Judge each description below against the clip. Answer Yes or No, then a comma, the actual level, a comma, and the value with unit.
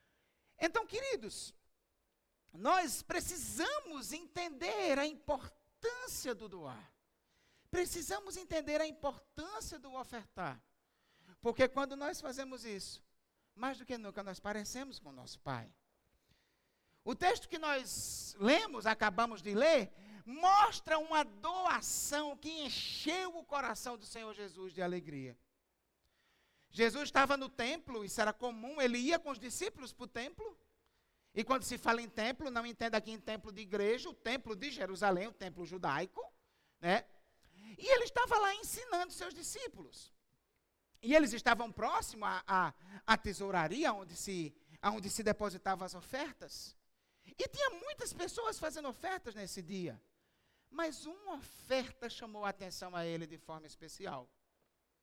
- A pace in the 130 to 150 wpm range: Yes, average, 140 wpm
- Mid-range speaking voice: No, high, 245 Hz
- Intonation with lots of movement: Yes, wide, 7.3 semitones